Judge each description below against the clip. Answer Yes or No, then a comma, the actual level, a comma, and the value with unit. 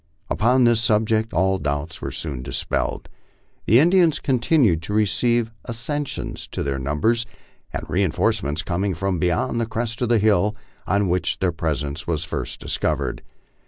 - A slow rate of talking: No, average, 155 wpm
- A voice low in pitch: Yes, low, 100 Hz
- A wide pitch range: Yes, wide, 6.1 semitones